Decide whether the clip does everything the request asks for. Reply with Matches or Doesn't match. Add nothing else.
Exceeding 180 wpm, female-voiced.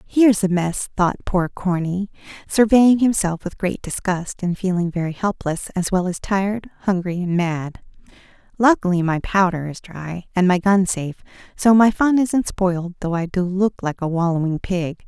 Doesn't match